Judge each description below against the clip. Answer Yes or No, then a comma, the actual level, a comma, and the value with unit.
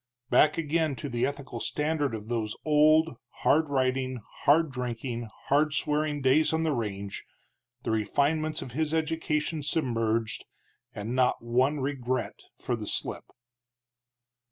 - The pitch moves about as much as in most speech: Yes, average, 4.4 semitones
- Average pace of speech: No, slow, 130 wpm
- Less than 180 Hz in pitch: Yes, medium, 140 Hz